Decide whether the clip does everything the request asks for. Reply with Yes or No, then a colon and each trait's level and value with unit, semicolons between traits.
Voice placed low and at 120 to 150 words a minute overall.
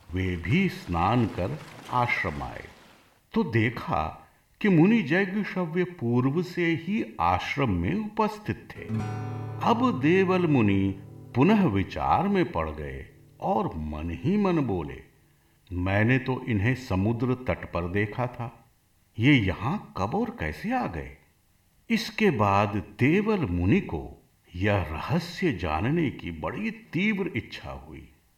Yes: low, 120 Hz; average, 125 wpm